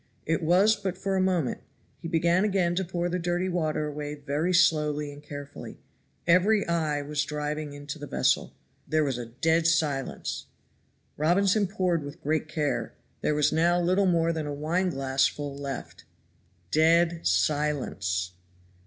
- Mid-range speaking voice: Yes, medium, 160 Hz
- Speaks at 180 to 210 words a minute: No, average, 155 wpm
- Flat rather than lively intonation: No, average, 3.2 semitones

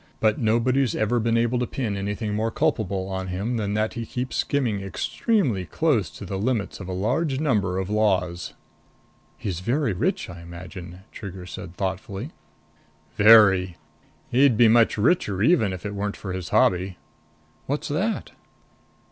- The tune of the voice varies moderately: Yes, average, 4.3 semitones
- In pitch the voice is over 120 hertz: No, low, 105 Hz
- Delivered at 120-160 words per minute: Yes, average, 155 wpm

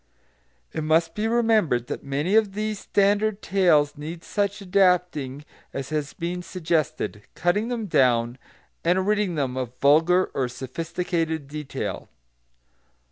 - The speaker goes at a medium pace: No, slow, 130 wpm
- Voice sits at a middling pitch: Yes, medium, 170 Hz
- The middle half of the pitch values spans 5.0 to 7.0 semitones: Yes, wide, 5.4 semitones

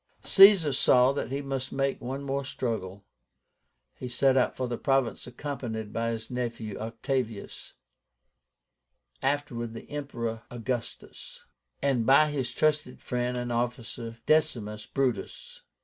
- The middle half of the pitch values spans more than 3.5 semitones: No, average, 3.0 semitones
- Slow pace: Yes, slow, 125 wpm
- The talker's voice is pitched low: Yes, low, 125 Hz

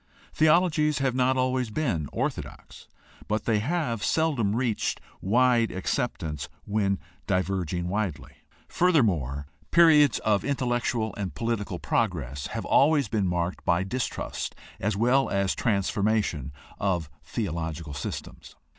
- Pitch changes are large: Yes, wide, 6.2 semitones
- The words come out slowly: Yes, slow, 115 wpm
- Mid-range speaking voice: No, low, 110 Hz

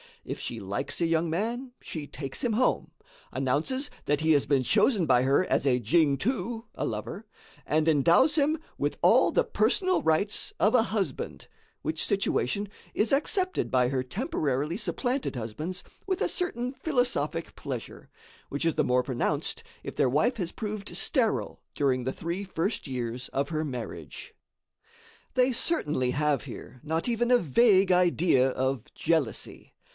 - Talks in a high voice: No, medium, 165 Hz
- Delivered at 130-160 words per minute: Yes, average, 155 wpm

